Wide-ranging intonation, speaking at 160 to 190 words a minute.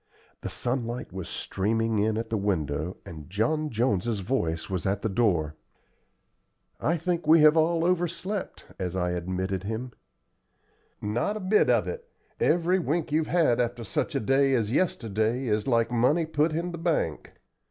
Yes: wide, 8.2 semitones; average, 170 wpm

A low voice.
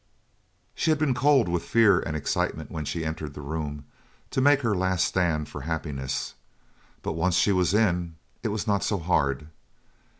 Yes: very low, 85 Hz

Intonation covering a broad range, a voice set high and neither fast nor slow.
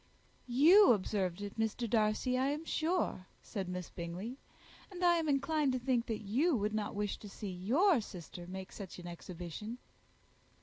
Yes: wide, 6.4 semitones; high, 220 Hz; average, 170 wpm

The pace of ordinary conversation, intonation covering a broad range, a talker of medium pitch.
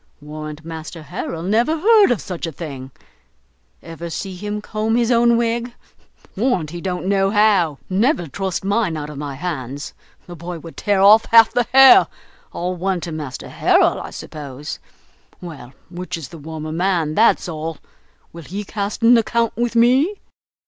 Yes: average, 170 wpm; wide, 5.9 semitones; medium, 180 Hz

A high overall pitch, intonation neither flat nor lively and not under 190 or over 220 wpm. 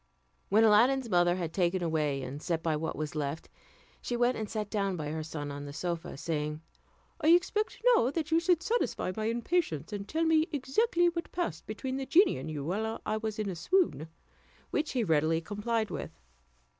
No: high, 205 Hz; wide, 9.0 semitones; average, 195 wpm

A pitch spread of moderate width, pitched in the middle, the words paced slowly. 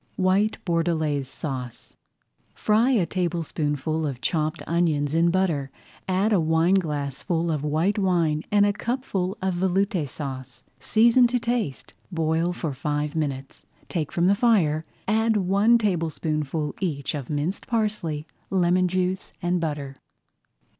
Yes: average, 4.4 semitones; medium, 170 Hz; slow, 130 wpm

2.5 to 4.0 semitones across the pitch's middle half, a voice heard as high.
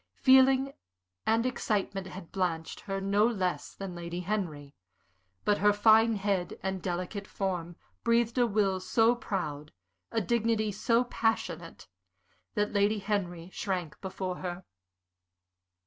Yes: average, 3.6 semitones; high, 195 Hz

